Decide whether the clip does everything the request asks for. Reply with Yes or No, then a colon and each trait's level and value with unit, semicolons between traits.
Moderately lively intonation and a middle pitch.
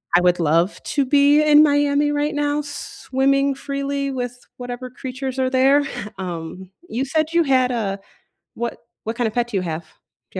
No: average, 3.6 semitones; very high, 260 Hz